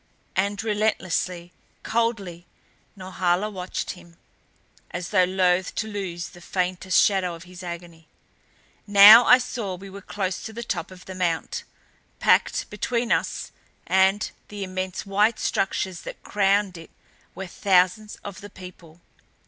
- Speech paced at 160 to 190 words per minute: No, average, 140 wpm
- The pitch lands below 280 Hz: Yes, high, 190 Hz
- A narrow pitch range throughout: Yes, narrow, 2.3 semitones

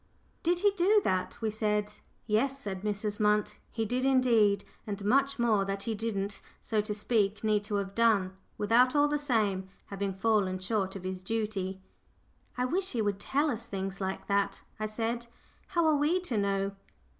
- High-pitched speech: Yes, high, 210 Hz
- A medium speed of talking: Yes, average, 180 wpm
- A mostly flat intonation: No, average, 3.7 semitones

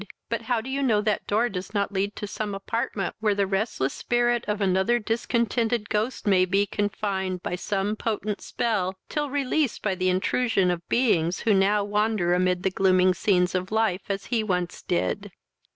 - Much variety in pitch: No, average, 3.3 semitones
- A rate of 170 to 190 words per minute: Yes, average, 185 wpm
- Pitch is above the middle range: Yes, high, 205 Hz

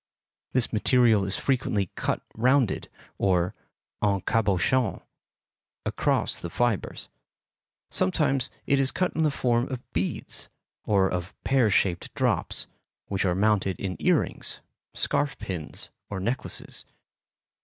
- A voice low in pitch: Yes, low, 105 Hz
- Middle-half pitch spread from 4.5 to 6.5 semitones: Yes, average, 5.1 semitones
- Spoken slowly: Yes, slow, 120 wpm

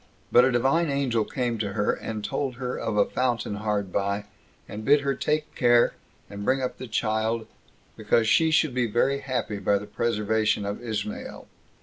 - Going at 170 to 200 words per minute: Yes, average, 185 wpm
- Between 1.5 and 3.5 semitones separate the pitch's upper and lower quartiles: No, average, 4.0 semitones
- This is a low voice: Yes, low, 115 Hz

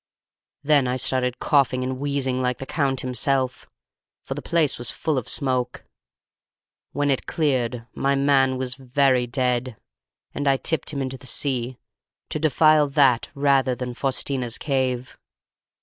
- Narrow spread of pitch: Yes, narrow, 1.8 semitones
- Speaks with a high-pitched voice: No, low, 130 Hz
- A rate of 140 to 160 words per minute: Yes, average, 150 wpm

